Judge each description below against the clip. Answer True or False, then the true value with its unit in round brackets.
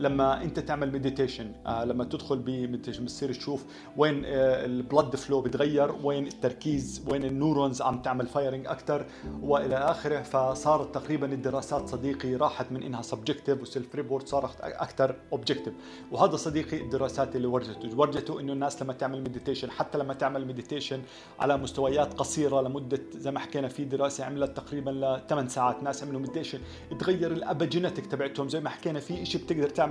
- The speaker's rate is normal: False (155 wpm)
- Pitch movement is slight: True (1.9 semitones)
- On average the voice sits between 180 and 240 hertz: False (140 Hz)